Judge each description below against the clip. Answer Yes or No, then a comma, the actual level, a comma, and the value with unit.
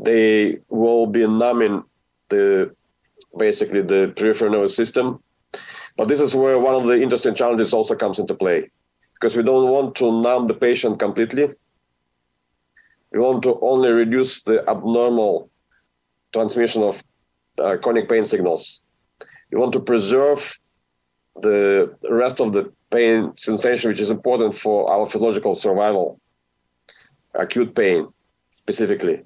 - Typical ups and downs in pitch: Yes, average, 5.0 semitones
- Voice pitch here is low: Yes, low, 115 Hz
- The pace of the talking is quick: No, slow, 135 wpm